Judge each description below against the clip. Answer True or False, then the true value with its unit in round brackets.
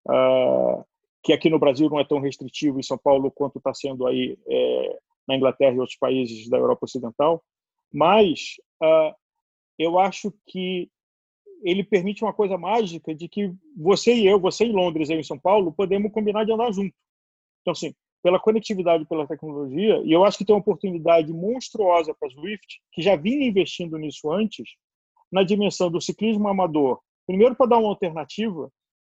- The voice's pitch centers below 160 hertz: False (185 Hz)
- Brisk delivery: False (175 wpm)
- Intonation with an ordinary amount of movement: False (5.8 semitones)